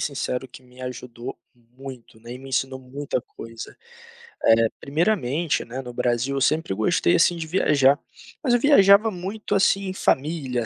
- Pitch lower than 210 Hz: Yes, low, 135 Hz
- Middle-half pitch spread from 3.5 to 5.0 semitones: No, wide, 5.6 semitones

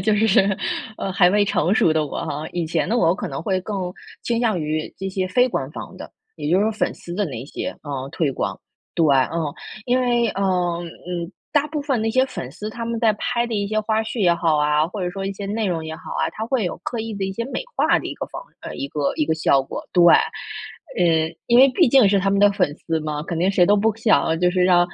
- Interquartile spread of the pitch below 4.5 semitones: No, average, 5.1 semitones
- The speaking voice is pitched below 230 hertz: Yes, high, 190 Hz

